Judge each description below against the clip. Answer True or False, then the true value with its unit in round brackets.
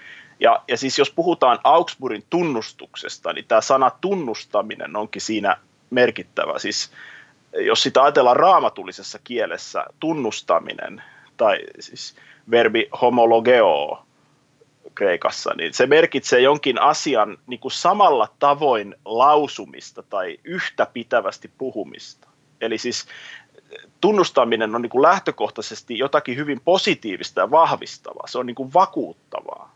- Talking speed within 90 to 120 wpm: True (115 wpm)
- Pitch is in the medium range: True (150 Hz)